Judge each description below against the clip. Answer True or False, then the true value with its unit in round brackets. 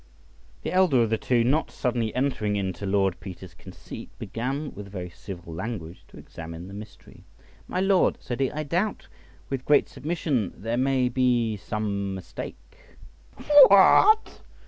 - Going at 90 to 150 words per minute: True (145 wpm)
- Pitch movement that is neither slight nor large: False (6.0 semitones)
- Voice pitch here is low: True (115 Hz)